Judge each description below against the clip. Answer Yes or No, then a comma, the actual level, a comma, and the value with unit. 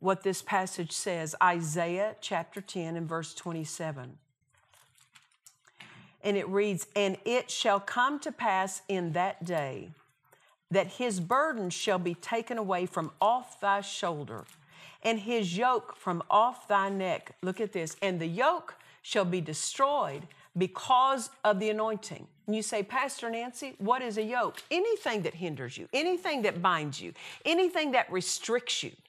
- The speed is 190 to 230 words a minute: No, average, 155 wpm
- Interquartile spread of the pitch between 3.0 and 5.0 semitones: No, wide, 5.4 semitones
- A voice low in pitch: No, high, 200 Hz